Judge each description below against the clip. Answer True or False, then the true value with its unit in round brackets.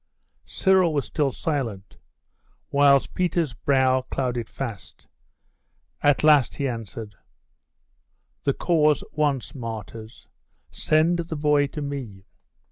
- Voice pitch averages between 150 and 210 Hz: False (140 Hz)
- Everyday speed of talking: False (105 wpm)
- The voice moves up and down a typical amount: True (4.2 semitones)